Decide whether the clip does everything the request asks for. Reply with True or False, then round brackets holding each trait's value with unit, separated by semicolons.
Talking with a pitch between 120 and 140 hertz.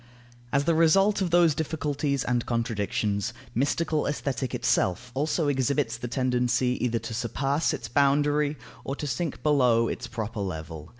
True (135 Hz)